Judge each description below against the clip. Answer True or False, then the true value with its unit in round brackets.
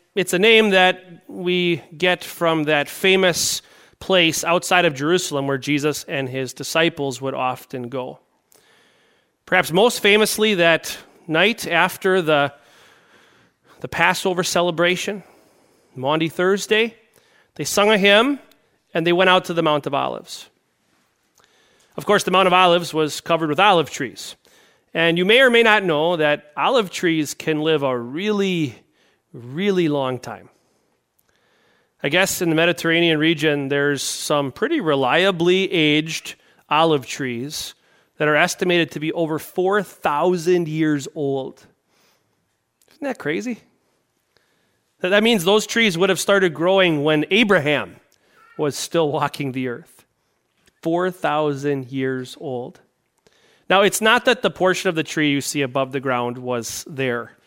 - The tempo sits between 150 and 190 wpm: False (140 wpm)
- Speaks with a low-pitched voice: False (165 Hz)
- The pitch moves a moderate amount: True (4.6 semitones)